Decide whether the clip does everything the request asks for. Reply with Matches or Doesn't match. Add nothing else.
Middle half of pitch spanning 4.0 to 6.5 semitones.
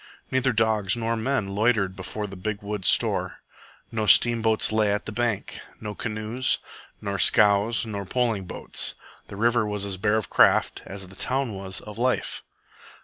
Doesn't match